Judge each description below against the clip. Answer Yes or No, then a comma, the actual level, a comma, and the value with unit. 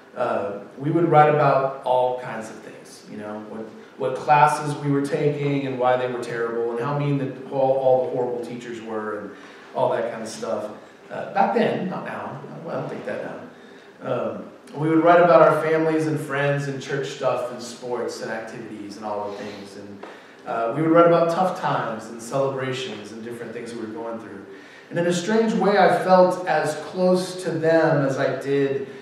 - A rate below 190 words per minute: No, fast, 205 wpm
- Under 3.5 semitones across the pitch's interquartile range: No, average, 5.1 semitones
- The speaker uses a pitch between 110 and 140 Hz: Yes, low, 135 Hz